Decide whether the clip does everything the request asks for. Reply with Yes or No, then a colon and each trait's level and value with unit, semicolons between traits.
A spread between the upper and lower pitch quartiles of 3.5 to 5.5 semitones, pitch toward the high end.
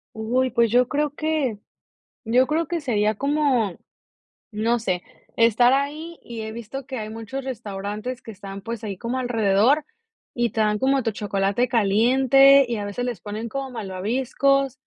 Yes: average, 4.0 semitones; high, 235 Hz